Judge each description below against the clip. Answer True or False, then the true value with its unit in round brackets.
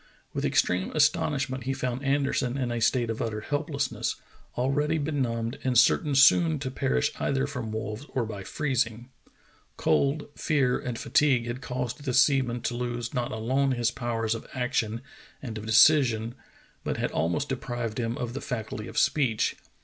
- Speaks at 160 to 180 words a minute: True (165 wpm)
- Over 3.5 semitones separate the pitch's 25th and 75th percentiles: False (3.1 semitones)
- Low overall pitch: True (125 Hz)